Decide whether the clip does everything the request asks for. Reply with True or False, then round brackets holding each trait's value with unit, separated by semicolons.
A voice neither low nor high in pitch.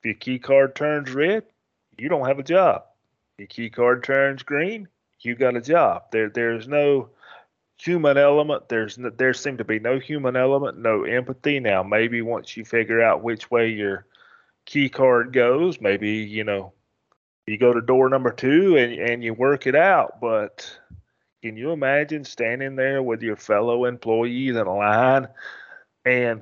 False (125 Hz)